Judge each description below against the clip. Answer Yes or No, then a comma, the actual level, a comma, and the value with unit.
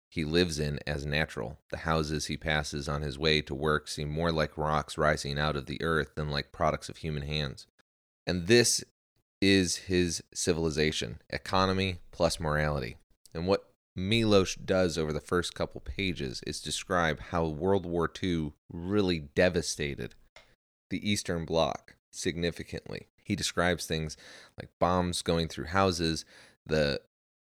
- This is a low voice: Yes, very low, 80 Hz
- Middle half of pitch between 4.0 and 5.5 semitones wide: No, average, 3.0 semitones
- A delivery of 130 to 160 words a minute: Yes, average, 145 wpm